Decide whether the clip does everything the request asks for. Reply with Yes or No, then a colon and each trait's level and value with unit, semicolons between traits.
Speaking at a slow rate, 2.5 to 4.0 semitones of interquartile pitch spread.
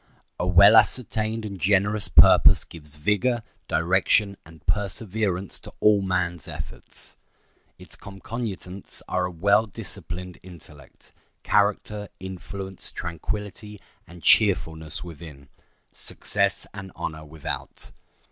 Yes: slow, 100 wpm; average, 3.2 semitones